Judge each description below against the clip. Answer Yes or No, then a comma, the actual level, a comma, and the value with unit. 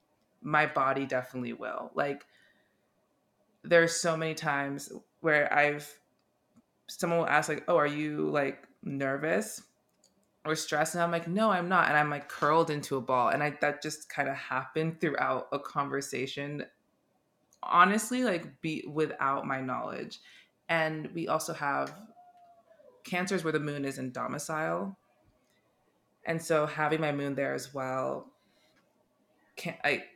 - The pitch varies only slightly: No, average, 3.3 semitones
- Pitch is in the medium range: Yes, medium, 150 Hz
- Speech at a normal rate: Yes, average, 145 wpm